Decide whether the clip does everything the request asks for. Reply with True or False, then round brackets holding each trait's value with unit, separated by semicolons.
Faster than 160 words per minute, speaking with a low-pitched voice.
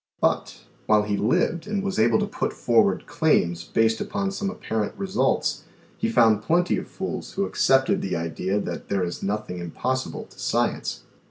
True (170 wpm; 110 Hz)